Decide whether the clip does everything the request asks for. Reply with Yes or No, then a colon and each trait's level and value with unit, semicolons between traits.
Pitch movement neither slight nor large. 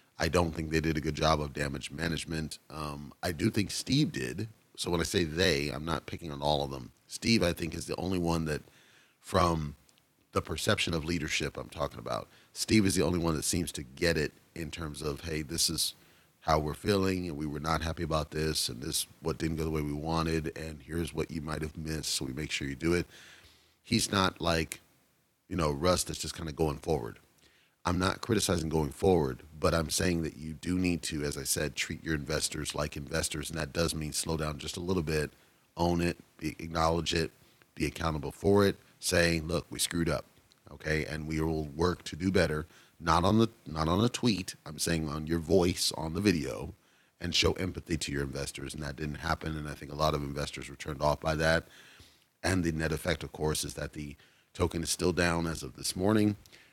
No: narrow, 2.2 semitones